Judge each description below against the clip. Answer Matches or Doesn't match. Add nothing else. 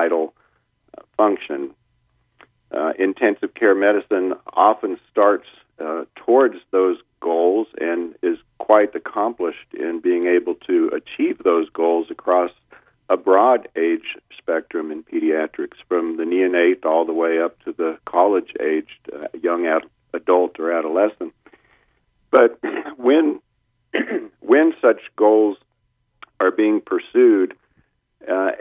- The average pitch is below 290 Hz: Doesn't match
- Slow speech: Matches